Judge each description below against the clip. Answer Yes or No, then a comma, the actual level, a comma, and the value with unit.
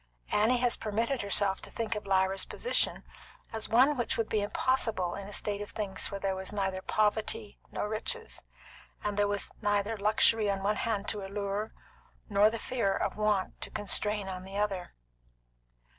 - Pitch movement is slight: Yes, narrow, 1.9 semitones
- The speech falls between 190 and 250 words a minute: No, average, 175 wpm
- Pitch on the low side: No, high, 205 Hz